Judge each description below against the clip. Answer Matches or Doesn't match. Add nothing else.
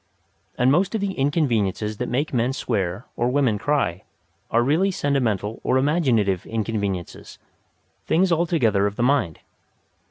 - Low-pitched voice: Matches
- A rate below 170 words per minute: Matches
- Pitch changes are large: Matches